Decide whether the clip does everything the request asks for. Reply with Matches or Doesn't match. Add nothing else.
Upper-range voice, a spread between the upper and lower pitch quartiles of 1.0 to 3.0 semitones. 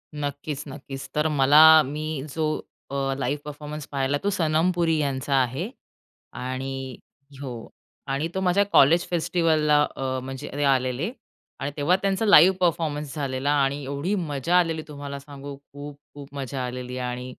Doesn't match